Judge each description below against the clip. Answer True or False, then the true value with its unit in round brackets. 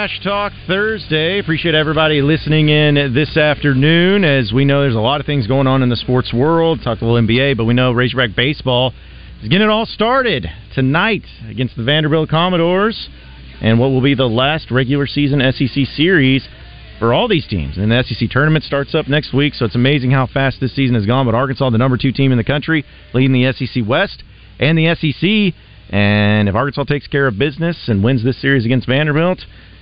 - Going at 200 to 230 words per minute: True (205 wpm)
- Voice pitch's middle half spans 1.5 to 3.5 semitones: False (4.1 semitones)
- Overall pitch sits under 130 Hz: False (135 Hz)